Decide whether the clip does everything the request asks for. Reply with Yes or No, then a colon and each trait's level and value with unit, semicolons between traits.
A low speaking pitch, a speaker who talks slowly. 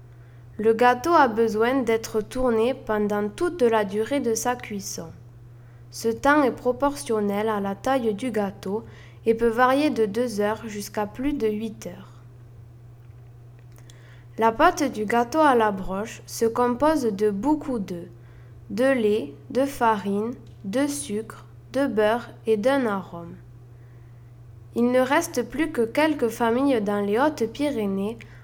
No: high, 220 Hz; slow, 140 wpm